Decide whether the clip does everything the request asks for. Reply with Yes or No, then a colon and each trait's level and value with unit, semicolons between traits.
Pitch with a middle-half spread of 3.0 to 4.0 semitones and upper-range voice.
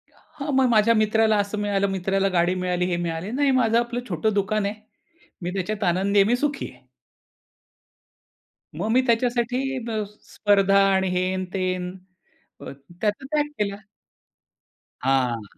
Yes: average, 3.7 semitones; high, 200 Hz